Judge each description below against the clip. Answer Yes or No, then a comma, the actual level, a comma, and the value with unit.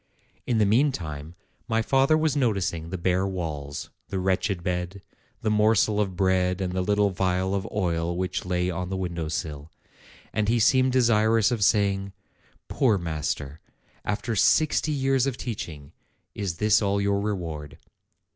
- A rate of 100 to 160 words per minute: Yes, average, 155 wpm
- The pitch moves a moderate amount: Yes, average, 3.6 semitones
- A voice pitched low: Yes, very low, 95 Hz